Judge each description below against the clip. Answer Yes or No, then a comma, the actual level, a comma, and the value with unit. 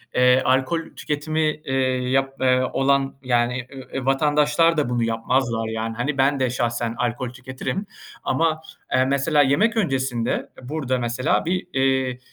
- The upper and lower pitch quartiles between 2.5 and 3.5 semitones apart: Yes, average, 2.9 semitones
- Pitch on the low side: Yes, low, 130 Hz